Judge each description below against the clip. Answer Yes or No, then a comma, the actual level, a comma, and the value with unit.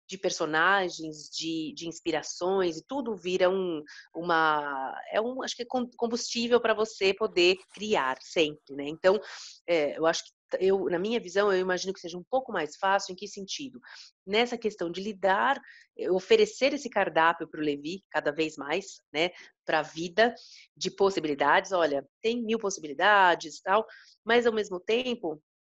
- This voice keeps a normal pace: Yes, average, 165 wpm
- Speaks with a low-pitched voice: No, high, 190 Hz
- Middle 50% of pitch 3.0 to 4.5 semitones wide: No, wide, 5.4 semitones